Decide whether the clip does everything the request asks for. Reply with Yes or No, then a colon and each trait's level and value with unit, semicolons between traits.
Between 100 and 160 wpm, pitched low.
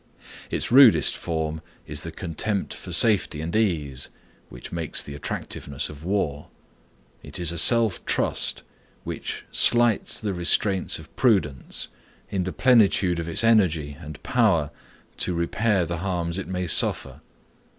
Yes: average, 140 wpm; very low, 90 Hz